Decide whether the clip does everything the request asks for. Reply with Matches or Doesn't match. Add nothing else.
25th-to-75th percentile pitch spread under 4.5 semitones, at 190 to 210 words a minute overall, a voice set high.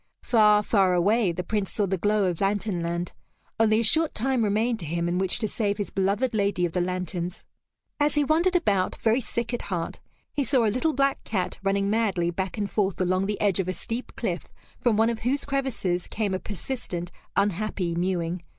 Matches